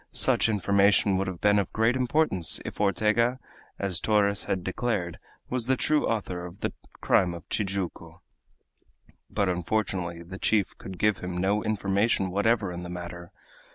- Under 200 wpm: Yes, average, 155 wpm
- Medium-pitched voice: No, low, 100 Hz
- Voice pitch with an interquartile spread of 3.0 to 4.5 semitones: Yes, average, 3.3 semitones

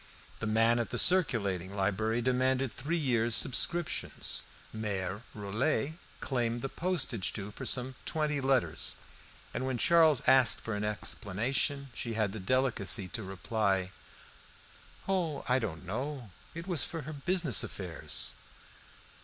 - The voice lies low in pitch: Yes, low, 120 Hz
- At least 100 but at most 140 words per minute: Yes, slow, 135 wpm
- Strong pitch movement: No, average, 5.0 semitones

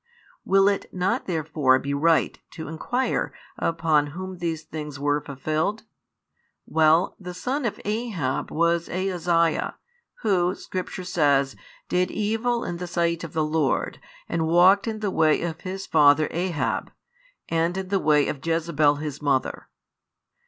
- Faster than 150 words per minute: No, average, 145 wpm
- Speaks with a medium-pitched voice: Yes, medium, 165 Hz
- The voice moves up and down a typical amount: Yes, average, 3.4 semitones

